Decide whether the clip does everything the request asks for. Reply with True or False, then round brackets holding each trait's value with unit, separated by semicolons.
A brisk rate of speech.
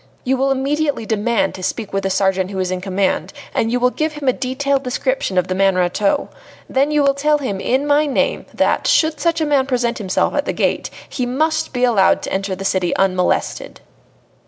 True (215 wpm)